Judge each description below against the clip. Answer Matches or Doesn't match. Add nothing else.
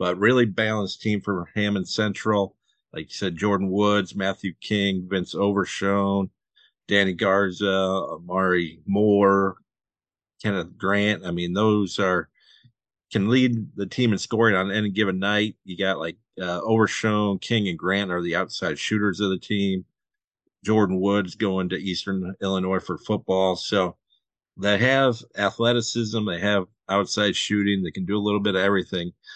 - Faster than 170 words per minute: Doesn't match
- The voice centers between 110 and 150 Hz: Doesn't match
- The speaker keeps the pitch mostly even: Matches